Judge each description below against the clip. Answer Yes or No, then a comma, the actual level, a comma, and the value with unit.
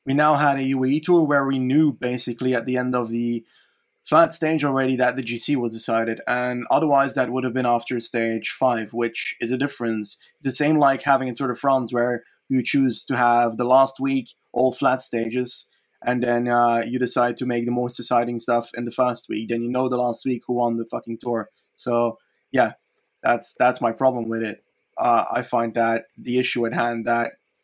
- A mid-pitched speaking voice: No, low, 125 Hz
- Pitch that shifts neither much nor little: No, narrow, 1.9 semitones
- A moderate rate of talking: No, fast, 215 wpm